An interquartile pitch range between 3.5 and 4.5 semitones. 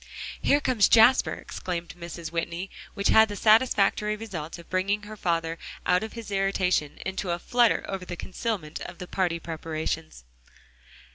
Yes: average, 3.9 semitones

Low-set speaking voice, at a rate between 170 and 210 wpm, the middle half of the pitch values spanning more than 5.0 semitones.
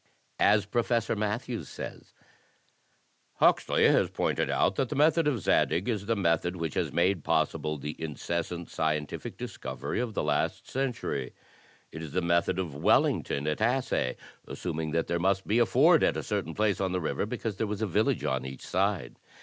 Yes: very low, 95 Hz; average, 180 wpm; wide, 5.5 semitones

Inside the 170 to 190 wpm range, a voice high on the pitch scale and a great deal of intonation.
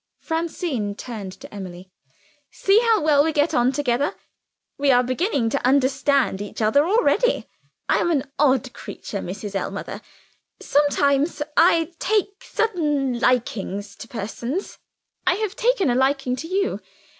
No: average, 140 wpm; very high, 280 Hz; wide, 5.8 semitones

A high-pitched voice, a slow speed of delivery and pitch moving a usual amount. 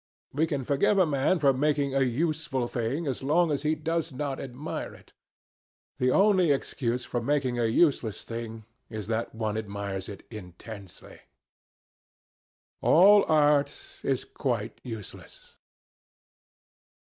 No: low, 135 Hz; slow, 130 wpm; average, 4.9 semitones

